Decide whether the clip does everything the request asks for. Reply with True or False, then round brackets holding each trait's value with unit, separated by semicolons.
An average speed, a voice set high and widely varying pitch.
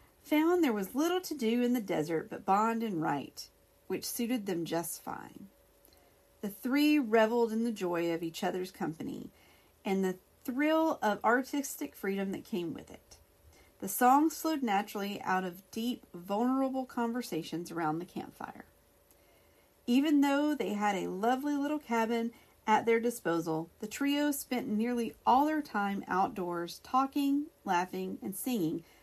True (150 wpm; 230 Hz; 6.4 semitones)